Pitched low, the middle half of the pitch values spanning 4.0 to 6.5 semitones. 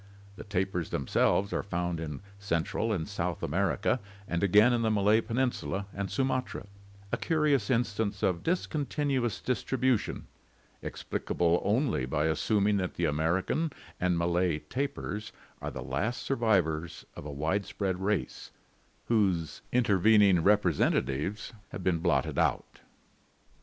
Yes: low, 100 Hz; average, 5.0 semitones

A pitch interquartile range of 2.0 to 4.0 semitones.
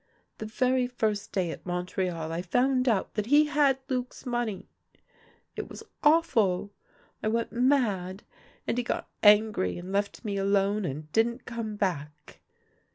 No: average, 4.8 semitones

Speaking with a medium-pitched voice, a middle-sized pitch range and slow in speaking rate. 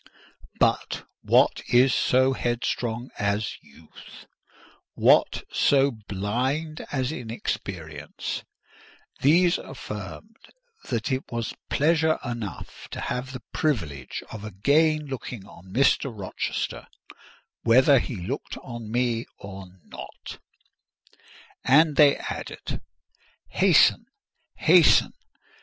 No: low, 120 Hz; average, 5.0 semitones; slow, 95 wpm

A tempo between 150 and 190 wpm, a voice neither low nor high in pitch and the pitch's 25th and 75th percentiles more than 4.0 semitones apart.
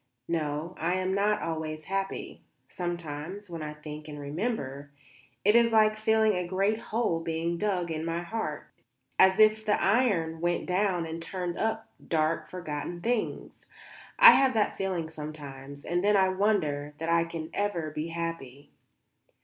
Yes: average, 155 wpm; medium, 170 Hz; average, 4.7 semitones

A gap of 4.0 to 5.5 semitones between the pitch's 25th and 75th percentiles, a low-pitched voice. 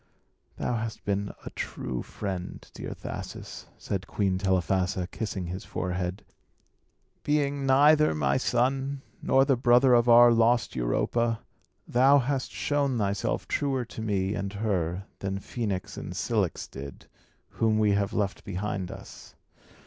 Yes: average, 4.7 semitones; low, 110 Hz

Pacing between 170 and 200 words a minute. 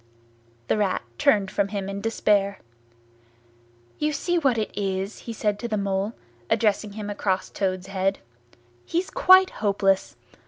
No: average, 145 wpm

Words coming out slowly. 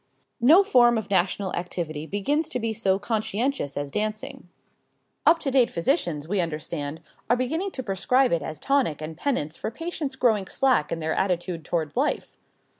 No: average, 170 wpm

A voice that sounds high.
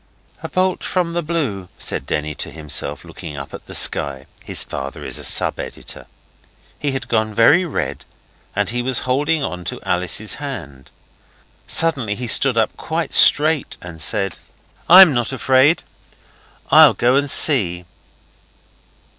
No: low, 120 Hz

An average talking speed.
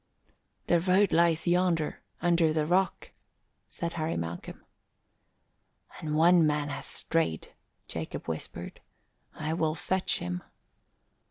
No: slow, 110 wpm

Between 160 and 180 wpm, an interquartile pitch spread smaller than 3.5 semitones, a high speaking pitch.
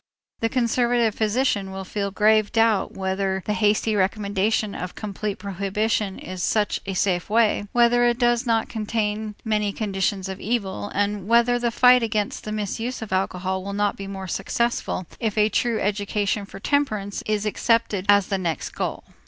Yes: average, 170 wpm; narrow, 2.5 semitones; high, 210 Hz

